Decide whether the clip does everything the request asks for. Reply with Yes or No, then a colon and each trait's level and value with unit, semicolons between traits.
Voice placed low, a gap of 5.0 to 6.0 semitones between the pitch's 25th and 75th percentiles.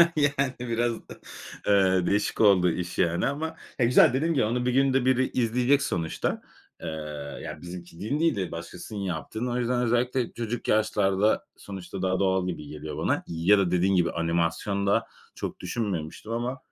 Yes: low, 105 Hz; wide, 5.5 semitones